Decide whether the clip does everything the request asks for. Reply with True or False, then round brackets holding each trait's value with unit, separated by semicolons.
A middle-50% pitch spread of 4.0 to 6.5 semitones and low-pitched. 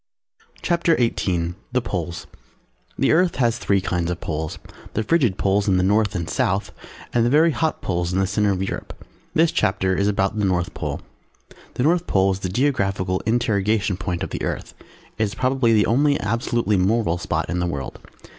True (4.5 semitones; 100 Hz)